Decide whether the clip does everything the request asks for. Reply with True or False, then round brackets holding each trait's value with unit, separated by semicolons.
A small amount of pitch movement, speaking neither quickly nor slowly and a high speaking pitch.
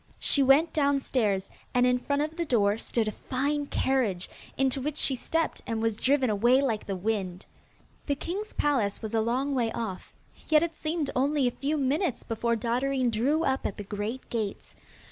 False (4.3 semitones; 185 wpm; 255 Hz)